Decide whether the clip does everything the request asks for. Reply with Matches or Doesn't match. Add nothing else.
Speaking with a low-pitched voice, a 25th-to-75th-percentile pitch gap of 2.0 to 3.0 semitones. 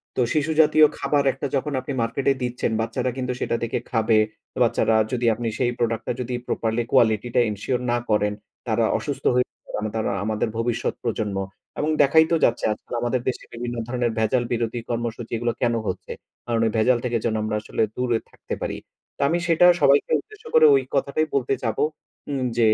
Matches